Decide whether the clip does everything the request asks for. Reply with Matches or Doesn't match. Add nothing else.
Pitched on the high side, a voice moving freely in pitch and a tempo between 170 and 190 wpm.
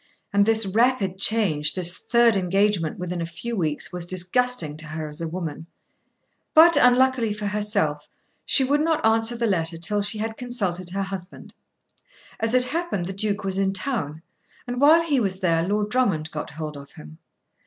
Matches